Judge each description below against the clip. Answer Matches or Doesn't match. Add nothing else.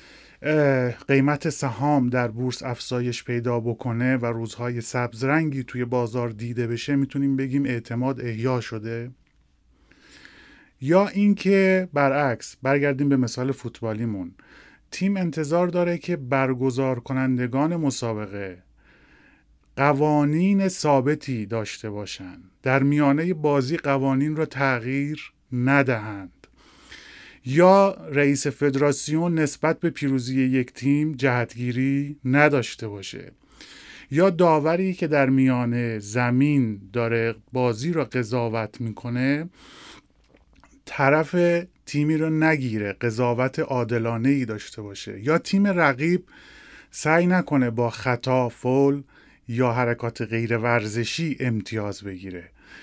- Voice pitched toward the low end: Matches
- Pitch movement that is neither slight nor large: Matches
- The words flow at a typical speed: Doesn't match